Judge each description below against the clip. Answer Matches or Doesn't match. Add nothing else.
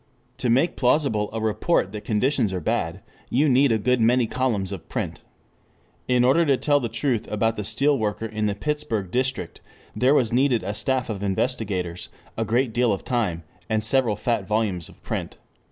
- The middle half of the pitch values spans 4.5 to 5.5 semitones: Doesn't match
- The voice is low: Matches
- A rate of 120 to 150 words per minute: Doesn't match